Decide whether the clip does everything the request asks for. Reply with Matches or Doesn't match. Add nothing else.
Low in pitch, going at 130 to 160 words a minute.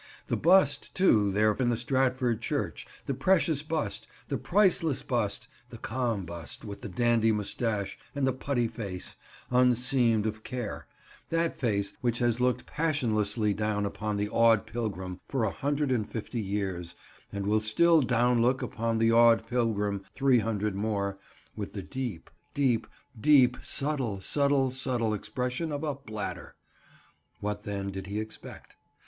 Matches